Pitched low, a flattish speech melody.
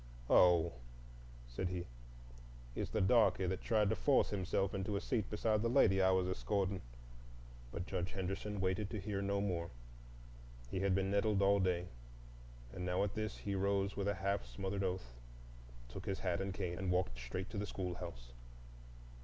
Yes: very low, 95 Hz; narrow, 1.8 semitones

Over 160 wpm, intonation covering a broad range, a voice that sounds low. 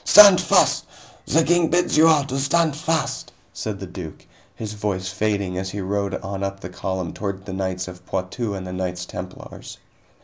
Yes: average, 190 wpm; wide, 6.6 semitones; low, 100 Hz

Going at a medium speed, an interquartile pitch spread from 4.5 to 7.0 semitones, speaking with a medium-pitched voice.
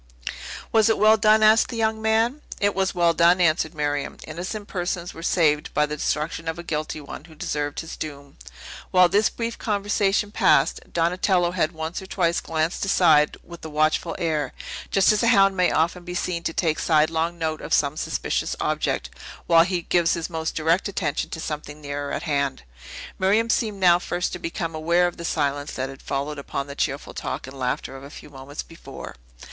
No: average, 195 wpm; average, 3.9 semitones; medium, 170 Hz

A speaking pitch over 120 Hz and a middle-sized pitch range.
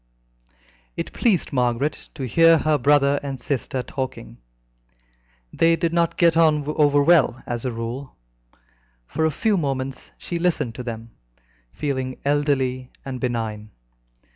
Yes: medium, 140 Hz; average, 3.7 semitones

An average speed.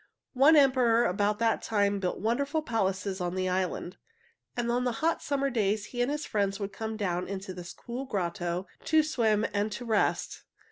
Yes: average, 180 wpm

